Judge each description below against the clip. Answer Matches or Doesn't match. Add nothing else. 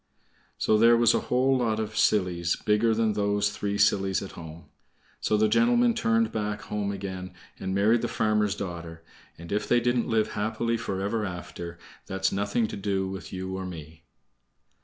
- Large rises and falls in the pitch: Doesn't match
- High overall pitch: Doesn't match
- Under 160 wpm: Doesn't match